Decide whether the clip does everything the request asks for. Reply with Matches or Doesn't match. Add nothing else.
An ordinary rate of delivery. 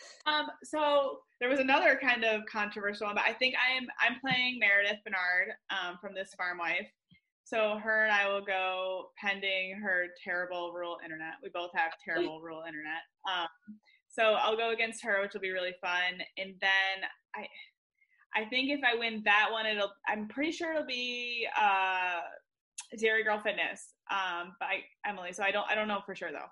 Matches